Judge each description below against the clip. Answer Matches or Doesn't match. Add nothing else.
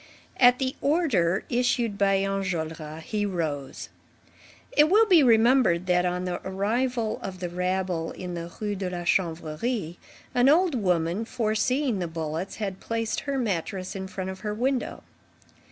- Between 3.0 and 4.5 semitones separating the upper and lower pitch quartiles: Doesn't match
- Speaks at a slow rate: Doesn't match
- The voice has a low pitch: Doesn't match